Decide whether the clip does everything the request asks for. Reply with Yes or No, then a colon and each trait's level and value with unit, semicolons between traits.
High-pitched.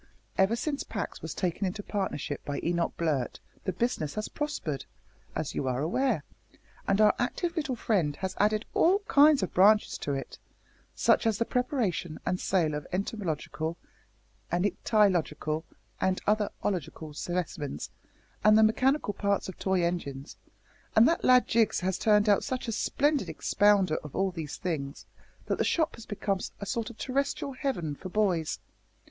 Yes: high, 195 Hz